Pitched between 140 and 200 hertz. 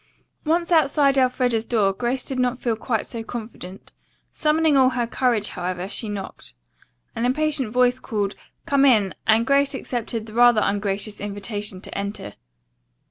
No: high, 235 Hz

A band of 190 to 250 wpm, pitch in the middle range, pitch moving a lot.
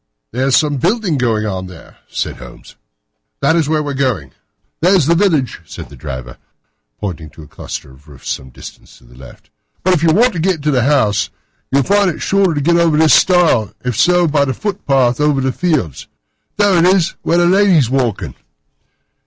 Yes: fast, 205 wpm; medium, 145 Hz; wide, 7.9 semitones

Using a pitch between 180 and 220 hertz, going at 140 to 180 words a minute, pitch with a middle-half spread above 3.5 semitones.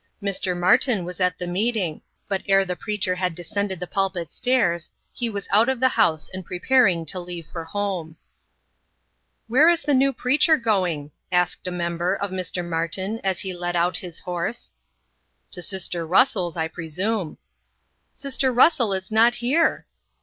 Yes: high, 190 Hz; average, 165 wpm; average, 4.5 semitones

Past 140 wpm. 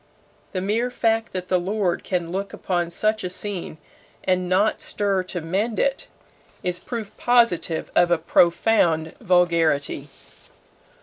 No: slow, 135 wpm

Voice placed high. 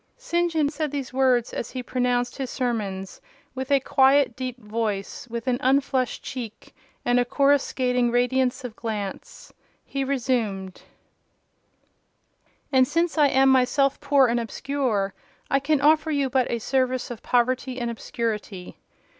Yes: very high, 255 Hz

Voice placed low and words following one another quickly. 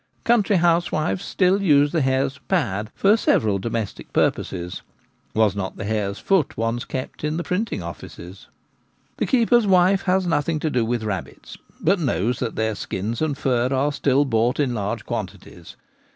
No: low, 130 Hz; average, 165 wpm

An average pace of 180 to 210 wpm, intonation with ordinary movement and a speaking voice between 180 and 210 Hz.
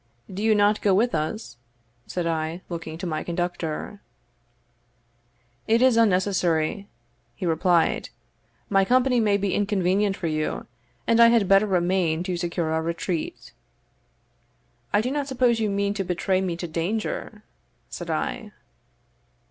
No: average, 140 wpm; average, 3.9 semitones; high, 190 Hz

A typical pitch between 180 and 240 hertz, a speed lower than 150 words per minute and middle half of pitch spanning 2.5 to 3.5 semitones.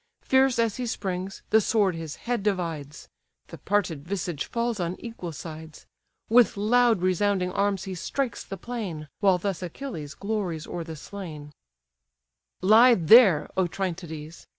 No: high, 190 Hz; average, 140 wpm; average, 4.9 semitones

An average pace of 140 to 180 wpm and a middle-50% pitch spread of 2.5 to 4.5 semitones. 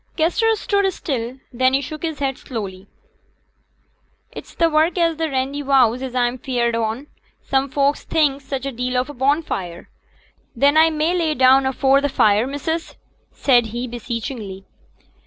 Yes: average, 160 wpm; average, 4.1 semitones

